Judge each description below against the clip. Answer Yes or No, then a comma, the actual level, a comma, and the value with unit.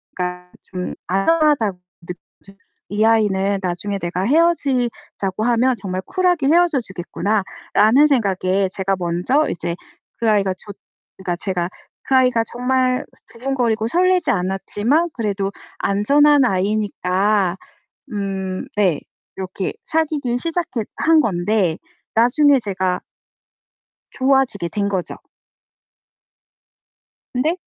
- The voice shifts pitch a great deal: Yes, wide, 5.7 semitones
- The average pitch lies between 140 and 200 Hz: No, high, 210 Hz